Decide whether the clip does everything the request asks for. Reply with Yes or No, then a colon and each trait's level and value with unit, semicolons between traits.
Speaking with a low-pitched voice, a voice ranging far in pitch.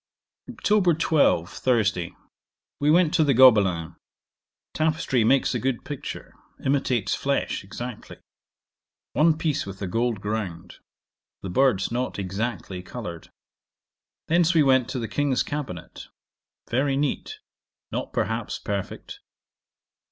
Yes: low, 125 Hz; wide, 6.7 semitones